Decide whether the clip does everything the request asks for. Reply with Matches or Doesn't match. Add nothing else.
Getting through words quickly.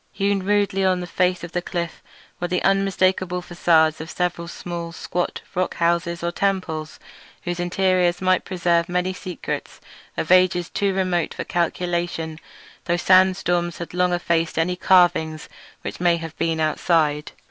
Doesn't match